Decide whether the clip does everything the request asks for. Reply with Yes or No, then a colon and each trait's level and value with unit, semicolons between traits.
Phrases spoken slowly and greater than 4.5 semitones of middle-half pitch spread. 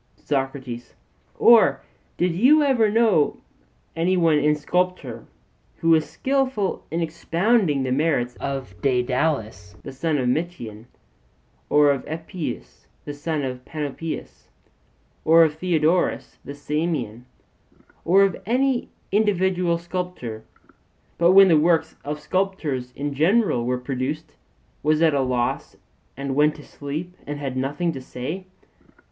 Yes: slow, 130 wpm; average, 5.0 semitones